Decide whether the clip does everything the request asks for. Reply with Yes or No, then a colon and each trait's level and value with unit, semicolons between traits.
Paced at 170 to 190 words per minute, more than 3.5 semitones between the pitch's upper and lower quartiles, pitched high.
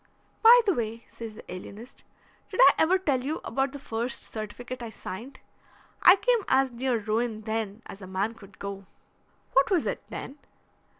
Yes: average, 175 wpm; average, 4.2 semitones; high, 235 Hz